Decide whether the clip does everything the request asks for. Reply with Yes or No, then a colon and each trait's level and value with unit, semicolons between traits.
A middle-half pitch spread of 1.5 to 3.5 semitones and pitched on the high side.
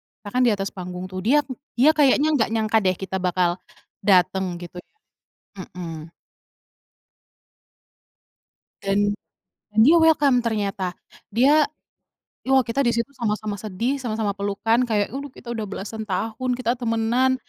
No: average, 4.2 semitones; high, 225 Hz